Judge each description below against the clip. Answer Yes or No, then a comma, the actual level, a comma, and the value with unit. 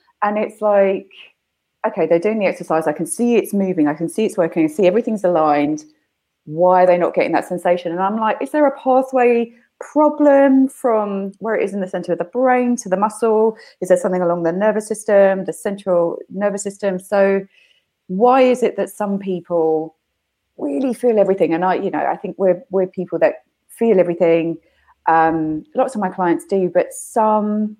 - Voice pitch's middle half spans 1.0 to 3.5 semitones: No, average, 4.1 semitones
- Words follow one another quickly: No, average, 195 wpm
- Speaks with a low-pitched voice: No, high, 195 Hz